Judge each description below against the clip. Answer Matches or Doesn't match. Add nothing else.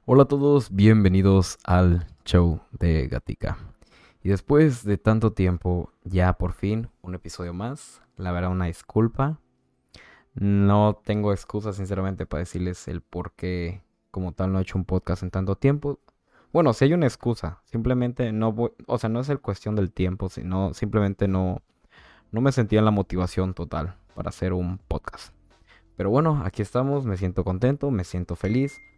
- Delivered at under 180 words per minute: Matches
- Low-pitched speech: Matches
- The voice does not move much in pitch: Doesn't match